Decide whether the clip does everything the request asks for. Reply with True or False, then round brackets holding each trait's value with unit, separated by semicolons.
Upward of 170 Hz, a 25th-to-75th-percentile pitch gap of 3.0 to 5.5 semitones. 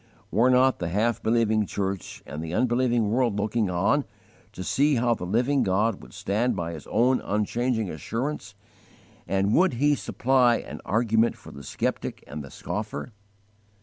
False (110 Hz; 4.2 semitones)